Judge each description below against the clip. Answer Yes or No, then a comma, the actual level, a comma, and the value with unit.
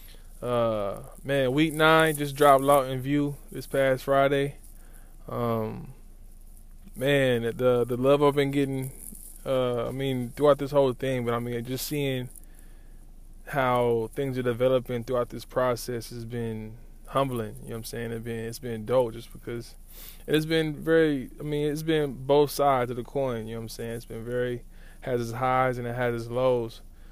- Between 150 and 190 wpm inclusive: Yes, average, 185 wpm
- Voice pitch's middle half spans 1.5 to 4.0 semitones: Yes, average, 3.1 semitones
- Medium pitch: No, low, 125 Hz